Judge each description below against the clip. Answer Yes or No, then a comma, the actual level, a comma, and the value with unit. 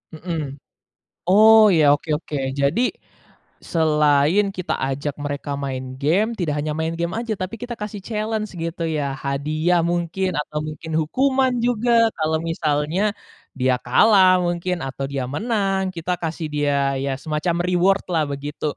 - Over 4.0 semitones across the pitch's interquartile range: Yes, average, 4.8 semitones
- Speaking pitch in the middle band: Yes, medium, 165 Hz